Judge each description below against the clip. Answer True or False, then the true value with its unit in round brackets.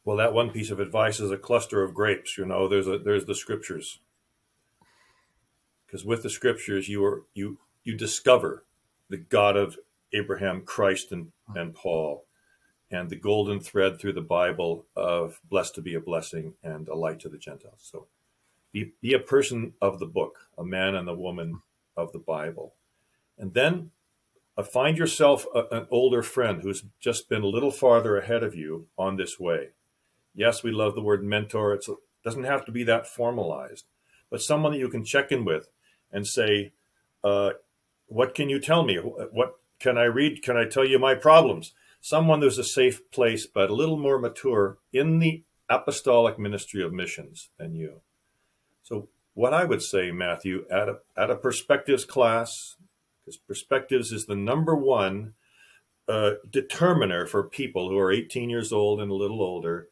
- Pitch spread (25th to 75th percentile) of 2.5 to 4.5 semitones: False (5.4 semitones)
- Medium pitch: False (110 Hz)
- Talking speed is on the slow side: False (180 wpm)